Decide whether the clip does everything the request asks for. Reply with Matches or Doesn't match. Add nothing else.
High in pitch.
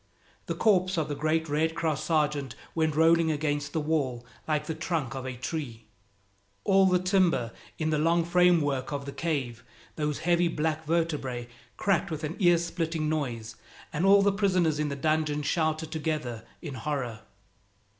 Doesn't match